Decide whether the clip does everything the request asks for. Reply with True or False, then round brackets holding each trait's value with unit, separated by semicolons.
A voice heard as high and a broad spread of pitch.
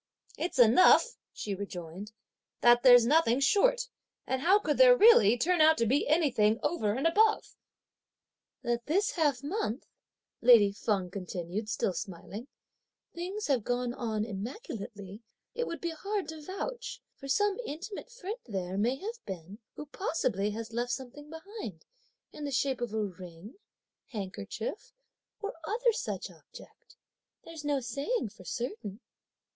True (255 Hz; 8.6 semitones)